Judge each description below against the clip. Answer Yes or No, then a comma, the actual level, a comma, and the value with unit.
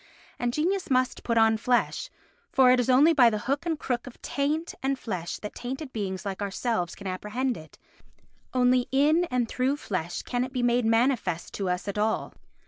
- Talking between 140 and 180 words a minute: No, average, 195 wpm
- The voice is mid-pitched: No, high, 245 Hz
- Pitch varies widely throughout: No, average, 4.2 semitones